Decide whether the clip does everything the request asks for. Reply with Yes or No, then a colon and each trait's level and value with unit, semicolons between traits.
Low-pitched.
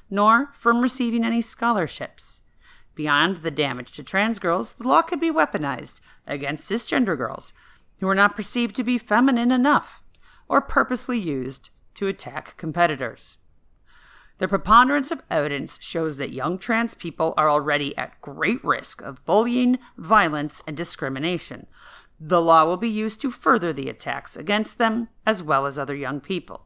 No: high, 195 Hz